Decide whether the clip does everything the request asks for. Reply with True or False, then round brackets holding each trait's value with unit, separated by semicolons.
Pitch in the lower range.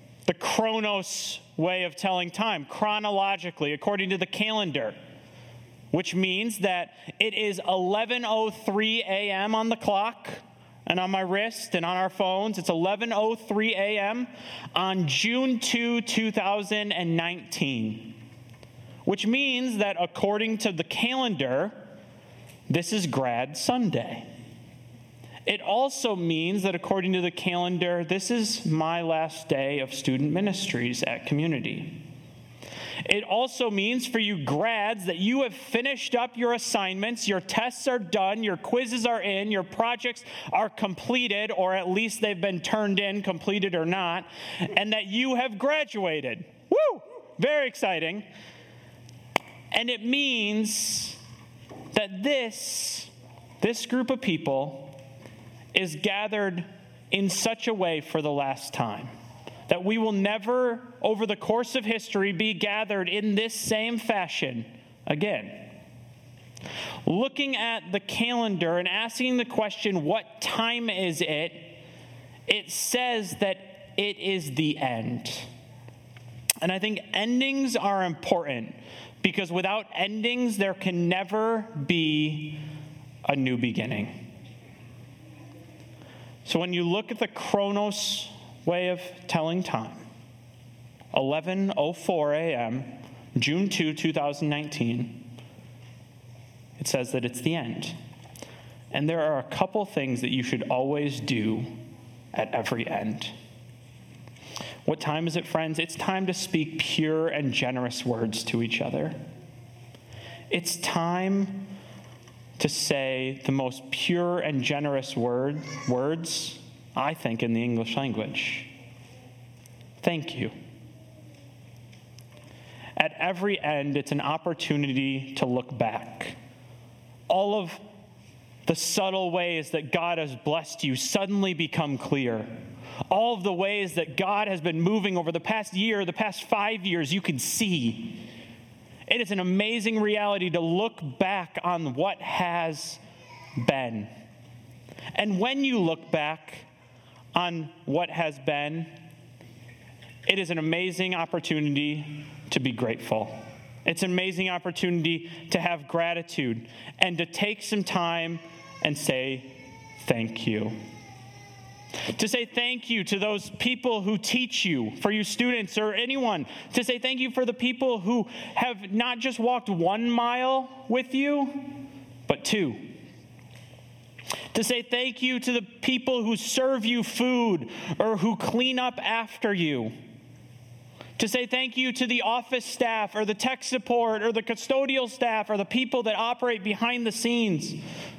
False (180 Hz)